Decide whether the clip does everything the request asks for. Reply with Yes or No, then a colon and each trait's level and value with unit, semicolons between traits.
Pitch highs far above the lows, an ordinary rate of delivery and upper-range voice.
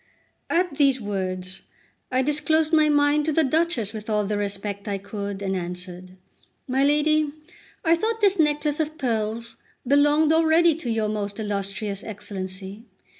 Yes: wide, 7.0 semitones; average, 155 wpm; high, 235 Hz